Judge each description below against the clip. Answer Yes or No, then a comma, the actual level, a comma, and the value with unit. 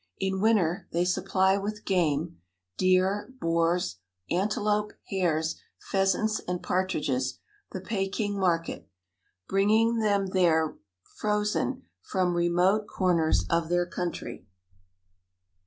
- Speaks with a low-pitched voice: No, medium, 185 Hz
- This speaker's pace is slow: Yes, slow, 100 wpm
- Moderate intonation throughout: Yes, average, 3.0 semitones